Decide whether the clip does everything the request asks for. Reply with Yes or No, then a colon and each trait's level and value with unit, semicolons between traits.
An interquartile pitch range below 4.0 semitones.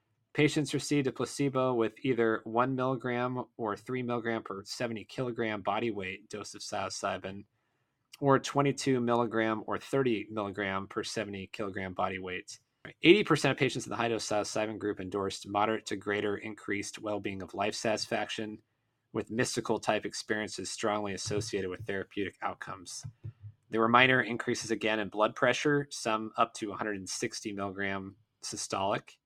Yes: average, 3.3 semitones